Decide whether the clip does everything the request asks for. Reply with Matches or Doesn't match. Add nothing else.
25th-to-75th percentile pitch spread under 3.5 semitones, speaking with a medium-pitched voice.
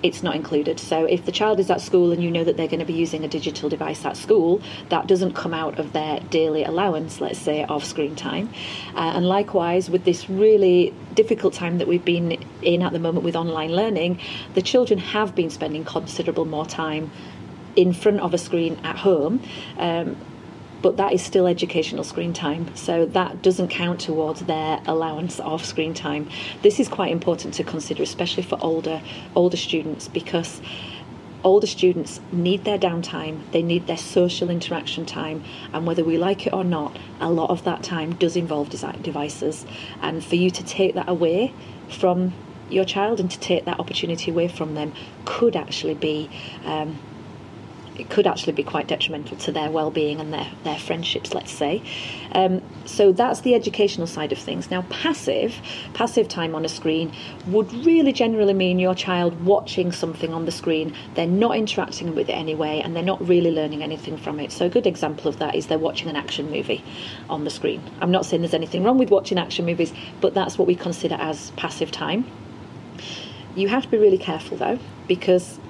Matches